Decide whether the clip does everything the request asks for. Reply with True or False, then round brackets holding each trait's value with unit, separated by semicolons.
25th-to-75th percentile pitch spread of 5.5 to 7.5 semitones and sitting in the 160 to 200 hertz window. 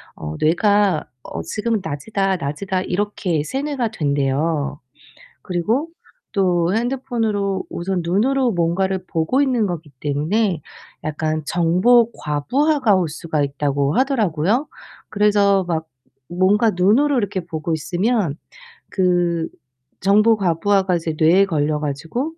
False (5.1 semitones; 185 Hz)